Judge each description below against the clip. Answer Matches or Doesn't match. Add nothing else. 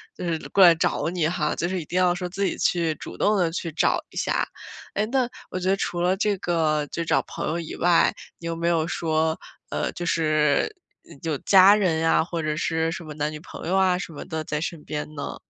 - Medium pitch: Matches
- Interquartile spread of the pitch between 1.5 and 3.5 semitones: Matches